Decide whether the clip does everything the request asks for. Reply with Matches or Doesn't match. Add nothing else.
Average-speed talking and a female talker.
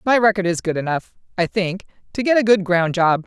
Doesn't match